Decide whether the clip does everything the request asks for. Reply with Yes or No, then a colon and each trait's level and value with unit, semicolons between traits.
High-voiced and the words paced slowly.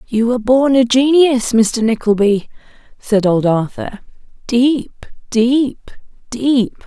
Yes: high, 235 Hz; slow, 115 wpm